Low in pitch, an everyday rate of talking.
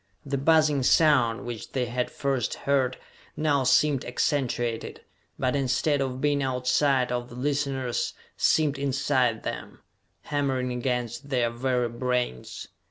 No: low, 130 Hz; slow, 125 wpm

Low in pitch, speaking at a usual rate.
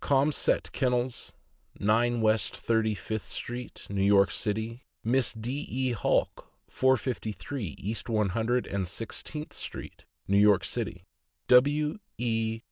No: low, 115 Hz; slow, 125 wpm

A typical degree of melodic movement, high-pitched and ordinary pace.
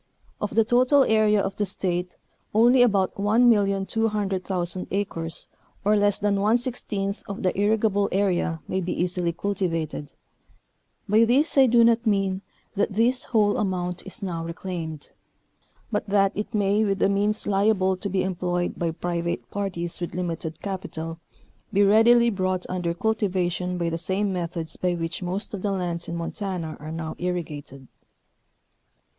Yes: average, 3.0 semitones; high, 195 Hz; average, 150 wpm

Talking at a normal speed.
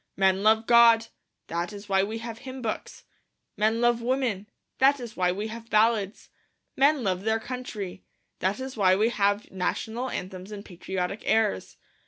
Yes: average, 165 wpm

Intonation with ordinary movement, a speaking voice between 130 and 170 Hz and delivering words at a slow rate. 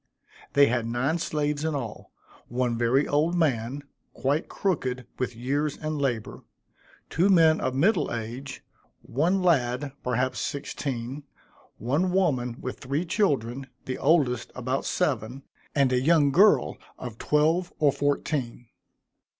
Yes: average, 4.0 semitones; medium, 140 Hz; slow, 130 wpm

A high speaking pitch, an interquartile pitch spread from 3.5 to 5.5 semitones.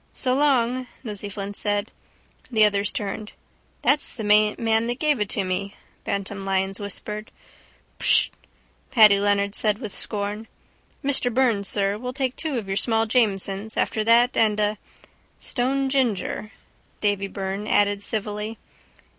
No: high, 210 Hz; average, 2.9 semitones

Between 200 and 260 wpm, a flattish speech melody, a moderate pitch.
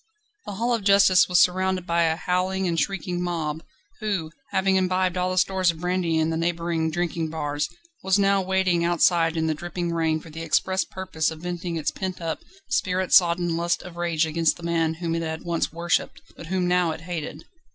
Yes: fast, 205 wpm; narrow, 2.1 semitones; medium, 175 Hz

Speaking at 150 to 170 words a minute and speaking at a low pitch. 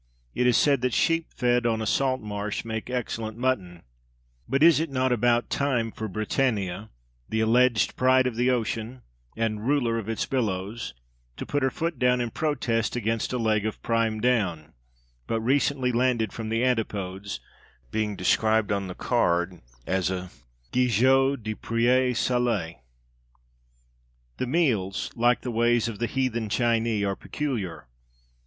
Yes: average, 155 wpm; low, 115 Hz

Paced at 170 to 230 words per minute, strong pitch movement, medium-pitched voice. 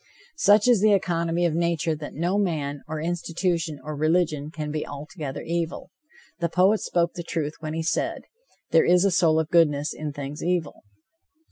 No: average, 175 wpm; narrow, 2.4 semitones; medium, 165 Hz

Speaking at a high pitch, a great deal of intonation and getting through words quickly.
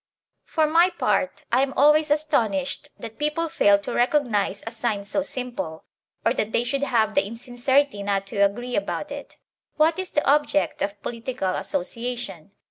No: high, 240 Hz; wide, 6.1 semitones; average, 165 wpm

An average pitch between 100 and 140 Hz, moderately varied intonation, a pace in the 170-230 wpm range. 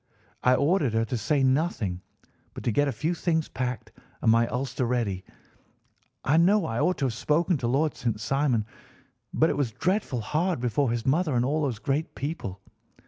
Yes: low, 135 Hz; average, 4.9 semitones; average, 190 wpm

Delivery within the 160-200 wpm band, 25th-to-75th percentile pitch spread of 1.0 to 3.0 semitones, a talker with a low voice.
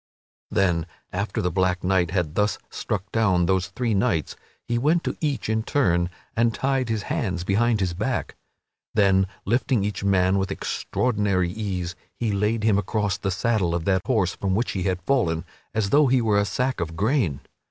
No: average, 185 wpm; average, 3.8 semitones; low, 100 Hz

